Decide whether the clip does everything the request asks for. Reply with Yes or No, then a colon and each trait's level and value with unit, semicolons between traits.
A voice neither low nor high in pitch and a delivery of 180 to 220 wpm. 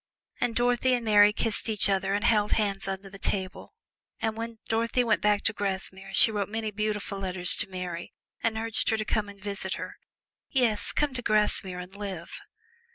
No: high, 210 Hz; average, 190 wpm